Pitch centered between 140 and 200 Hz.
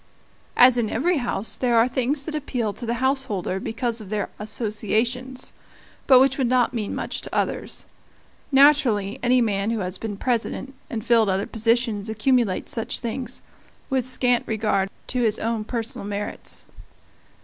No: high, 235 Hz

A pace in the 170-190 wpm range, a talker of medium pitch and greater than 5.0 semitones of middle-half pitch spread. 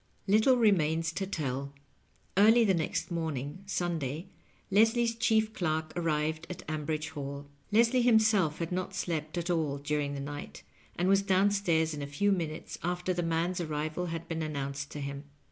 No: average, 180 wpm; medium, 165 Hz; average, 4.3 semitones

